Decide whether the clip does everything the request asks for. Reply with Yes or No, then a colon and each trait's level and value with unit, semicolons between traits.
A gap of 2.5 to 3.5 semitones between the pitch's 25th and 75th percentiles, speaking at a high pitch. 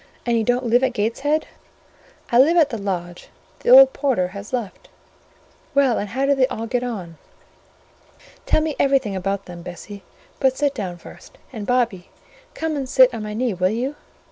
No: average, 5.3 semitones; high, 240 Hz